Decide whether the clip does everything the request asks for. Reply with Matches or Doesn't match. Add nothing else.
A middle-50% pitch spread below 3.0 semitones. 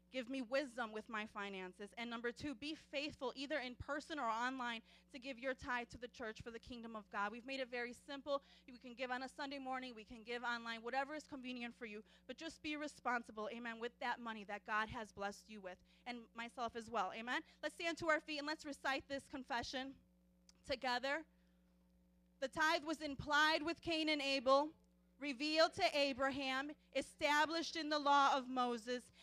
Doesn't match